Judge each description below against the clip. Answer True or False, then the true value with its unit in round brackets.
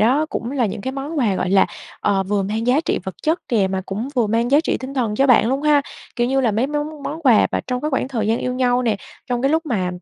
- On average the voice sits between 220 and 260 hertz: True (250 Hz)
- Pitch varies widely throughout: False (4.3 semitones)